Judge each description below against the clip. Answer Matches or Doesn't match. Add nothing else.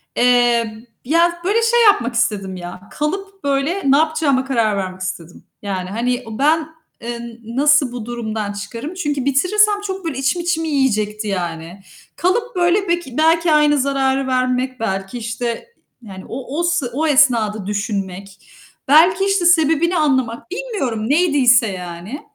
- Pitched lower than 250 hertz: Doesn't match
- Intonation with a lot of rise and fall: Matches